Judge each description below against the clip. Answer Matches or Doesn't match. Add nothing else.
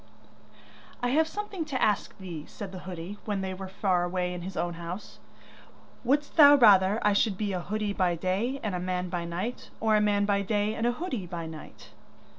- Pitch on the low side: Doesn't match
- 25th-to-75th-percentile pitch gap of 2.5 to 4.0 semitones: Matches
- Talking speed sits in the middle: Doesn't match